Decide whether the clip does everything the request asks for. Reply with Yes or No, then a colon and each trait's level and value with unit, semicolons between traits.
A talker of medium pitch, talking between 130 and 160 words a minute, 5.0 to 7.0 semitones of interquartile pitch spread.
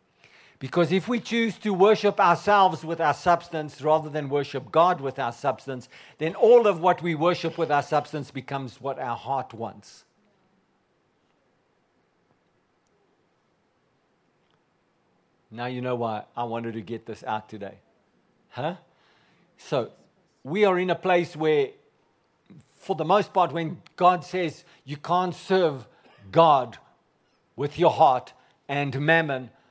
Yes: medium, 155 Hz; slow, 135 wpm; average, 5.3 semitones